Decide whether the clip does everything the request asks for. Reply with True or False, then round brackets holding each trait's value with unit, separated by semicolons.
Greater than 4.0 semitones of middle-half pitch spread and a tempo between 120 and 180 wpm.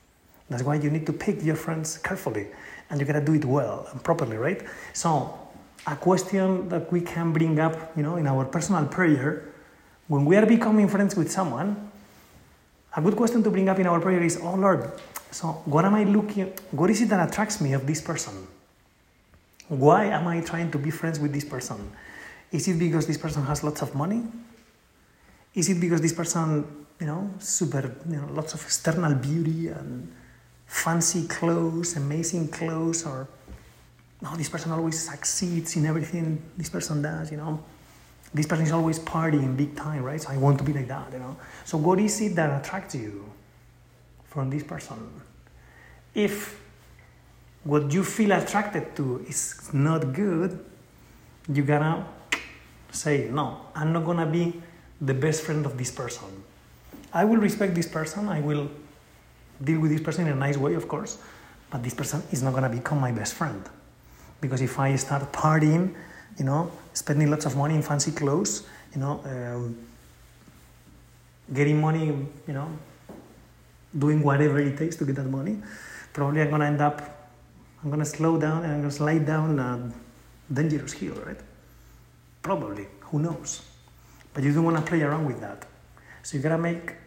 False (3.2 semitones; 175 wpm)